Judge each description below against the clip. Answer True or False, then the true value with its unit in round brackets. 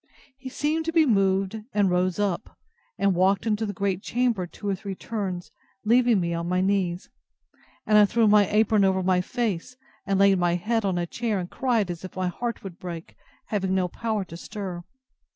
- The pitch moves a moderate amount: True (3.3 semitones)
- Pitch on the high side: True (195 Hz)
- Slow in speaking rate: False (200 wpm)